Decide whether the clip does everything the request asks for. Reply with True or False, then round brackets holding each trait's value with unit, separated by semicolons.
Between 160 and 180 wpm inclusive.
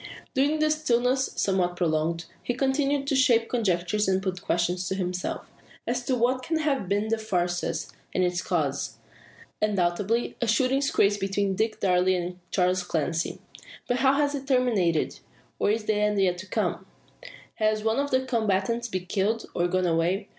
True (170 wpm)